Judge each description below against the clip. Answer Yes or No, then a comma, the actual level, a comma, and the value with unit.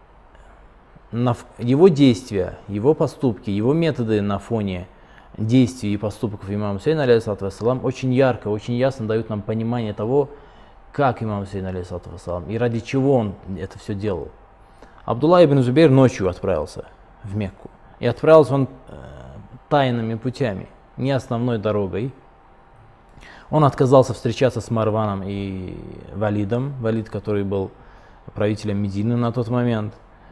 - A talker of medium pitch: No, low, 115 Hz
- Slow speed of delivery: No, average, 125 wpm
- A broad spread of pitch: No, average, 4.2 semitones